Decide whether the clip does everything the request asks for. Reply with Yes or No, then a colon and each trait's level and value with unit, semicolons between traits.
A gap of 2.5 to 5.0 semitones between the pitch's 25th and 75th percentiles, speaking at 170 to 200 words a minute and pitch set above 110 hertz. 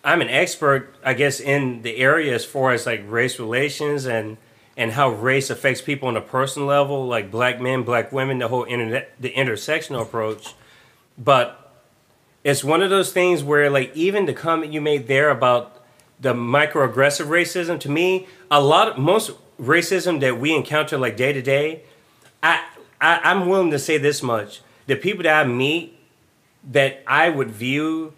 Yes: average, 3.5 semitones; average, 175 wpm; medium, 140 Hz